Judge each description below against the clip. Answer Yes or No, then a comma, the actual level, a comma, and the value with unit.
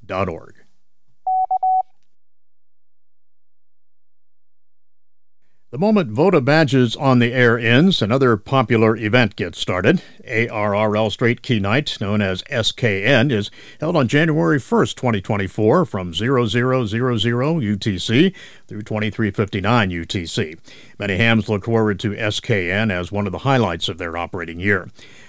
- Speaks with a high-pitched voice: No, low, 110 Hz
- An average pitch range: Yes, average, 4.0 semitones